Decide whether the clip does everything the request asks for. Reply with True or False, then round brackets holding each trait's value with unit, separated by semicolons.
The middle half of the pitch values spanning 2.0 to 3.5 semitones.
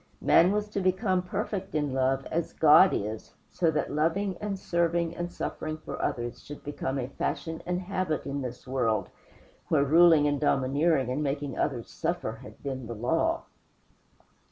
False (4.7 semitones)